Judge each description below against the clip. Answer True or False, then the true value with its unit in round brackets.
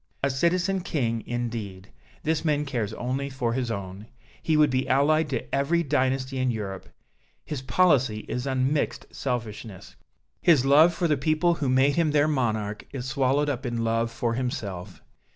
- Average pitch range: True (4.2 semitones)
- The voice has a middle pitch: False (130 Hz)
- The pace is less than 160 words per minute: False (165 wpm)